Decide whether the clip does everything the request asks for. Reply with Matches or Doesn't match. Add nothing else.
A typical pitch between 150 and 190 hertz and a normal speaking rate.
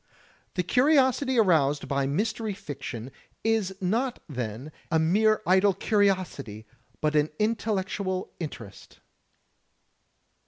Doesn't match